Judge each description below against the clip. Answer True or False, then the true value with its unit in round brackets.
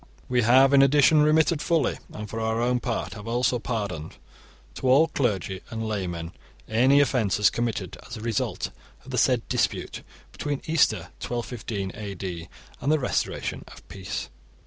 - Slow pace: False (155 wpm)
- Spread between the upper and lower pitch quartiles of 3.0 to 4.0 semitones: False (4.8 semitones)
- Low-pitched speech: True (120 Hz)